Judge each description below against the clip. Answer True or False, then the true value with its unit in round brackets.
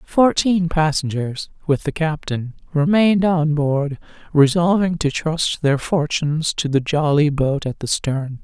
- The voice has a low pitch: False (155 Hz)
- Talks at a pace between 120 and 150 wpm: True (140 wpm)